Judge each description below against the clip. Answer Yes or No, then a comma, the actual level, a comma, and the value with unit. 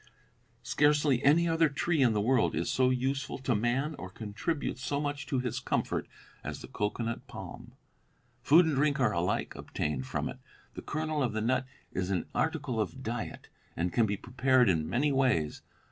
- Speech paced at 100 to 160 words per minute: No, average, 180 wpm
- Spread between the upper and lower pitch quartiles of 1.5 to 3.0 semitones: No, average, 4.8 semitones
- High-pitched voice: No, low, 130 Hz